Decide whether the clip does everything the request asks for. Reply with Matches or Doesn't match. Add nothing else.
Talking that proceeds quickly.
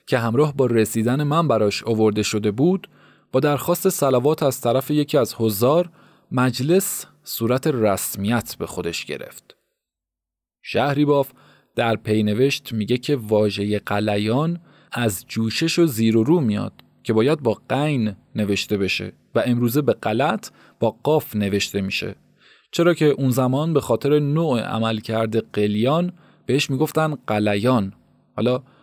Doesn't match